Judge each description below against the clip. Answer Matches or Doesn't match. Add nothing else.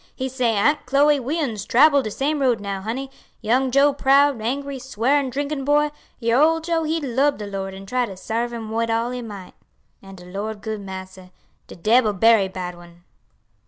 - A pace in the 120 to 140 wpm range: Doesn't match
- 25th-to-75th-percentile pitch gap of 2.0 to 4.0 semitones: Doesn't match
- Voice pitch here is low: Doesn't match